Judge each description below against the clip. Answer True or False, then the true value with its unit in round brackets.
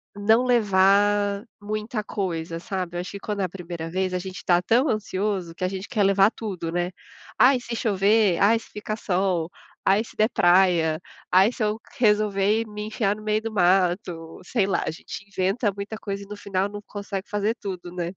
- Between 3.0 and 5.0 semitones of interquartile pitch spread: False (2.6 semitones)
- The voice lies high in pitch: True (200 Hz)